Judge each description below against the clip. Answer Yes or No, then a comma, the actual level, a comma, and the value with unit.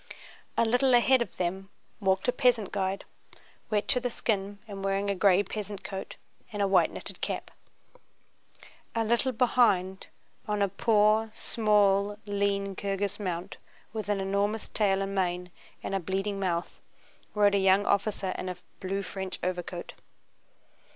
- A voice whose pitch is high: Yes, high, 200 Hz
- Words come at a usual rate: Yes, average, 150 wpm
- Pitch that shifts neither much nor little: No, narrow, 1.8 semitones